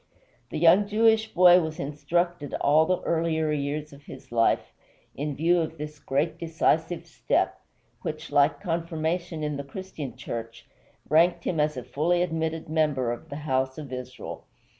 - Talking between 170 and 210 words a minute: No, average, 160 wpm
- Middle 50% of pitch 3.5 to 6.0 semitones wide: No, average, 3.0 semitones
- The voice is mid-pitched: Yes, medium, 155 Hz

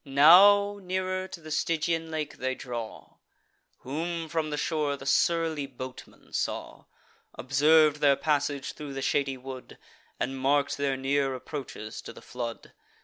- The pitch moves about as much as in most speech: Yes, average, 3.3 semitones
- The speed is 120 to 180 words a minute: Yes, average, 145 wpm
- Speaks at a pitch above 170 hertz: No, medium, 145 Hz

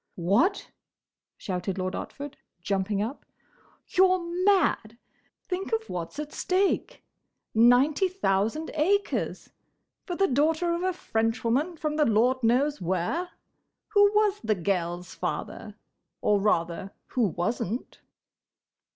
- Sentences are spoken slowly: Yes, slow, 110 wpm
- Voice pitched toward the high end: Yes, very high, 260 Hz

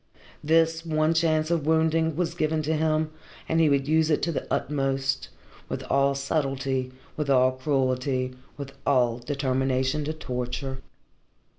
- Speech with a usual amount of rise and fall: Yes, average, 3.1 semitones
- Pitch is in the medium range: Yes, medium, 145 Hz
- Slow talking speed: No, average, 145 wpm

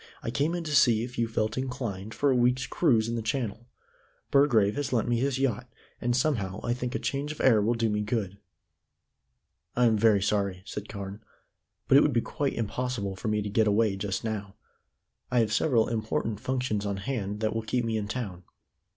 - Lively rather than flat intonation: No, average, 3.3 semitones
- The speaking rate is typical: No, fast, 210 wpm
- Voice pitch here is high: No, low, 115 Hz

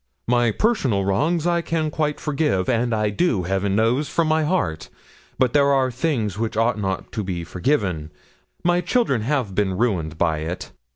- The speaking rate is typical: Yes, average, 175 wpm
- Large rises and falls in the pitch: Yes, wide, 7.7 semitones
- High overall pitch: No, low, 115 Hz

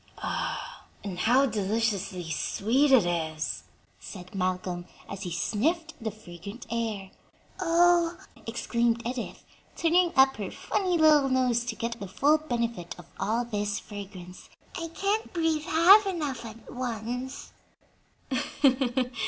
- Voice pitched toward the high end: Yes, high, 235 Hz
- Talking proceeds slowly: Yes, slow, 120 wpm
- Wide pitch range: Yes, wide, 7.4 semitones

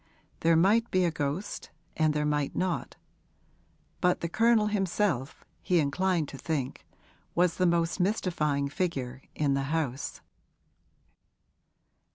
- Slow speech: Yes, slow, 125 wpm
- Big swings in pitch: No, average, 4.4 semitones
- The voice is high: No, medium, 165 Hz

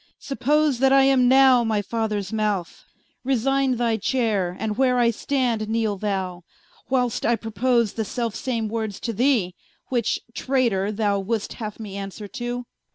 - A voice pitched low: No, high, 230 Hz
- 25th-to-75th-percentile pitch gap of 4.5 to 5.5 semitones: No, average, 3.3 semitones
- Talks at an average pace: Yes, average, 160 wpm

